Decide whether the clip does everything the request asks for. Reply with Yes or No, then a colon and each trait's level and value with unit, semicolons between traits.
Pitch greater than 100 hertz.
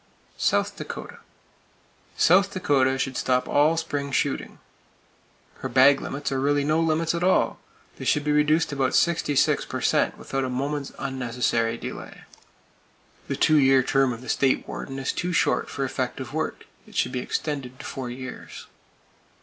Yes: low, 135 Hz